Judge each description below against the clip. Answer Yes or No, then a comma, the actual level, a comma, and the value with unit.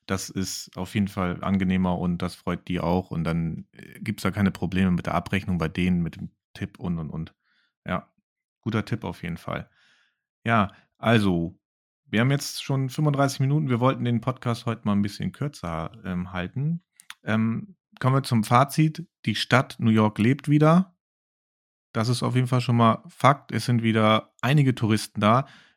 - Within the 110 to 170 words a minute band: No, average, 185 wpm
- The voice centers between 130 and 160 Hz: No, low, 110 Hz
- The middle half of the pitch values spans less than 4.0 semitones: No, wide, 6.0 semitones